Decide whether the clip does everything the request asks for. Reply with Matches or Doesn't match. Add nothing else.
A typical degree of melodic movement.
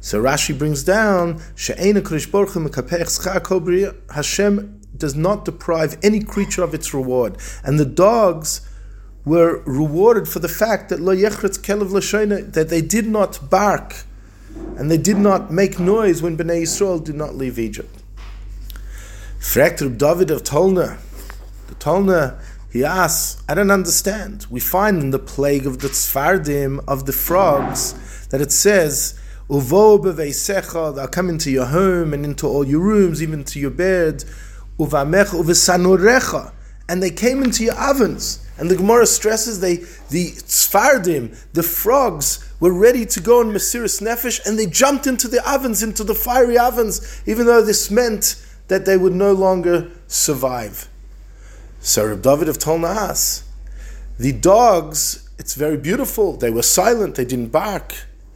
Doesn't match